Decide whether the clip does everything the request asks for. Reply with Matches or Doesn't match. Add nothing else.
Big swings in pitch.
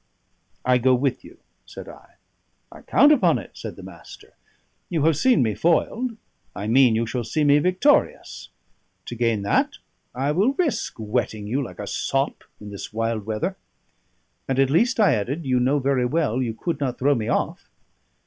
Matches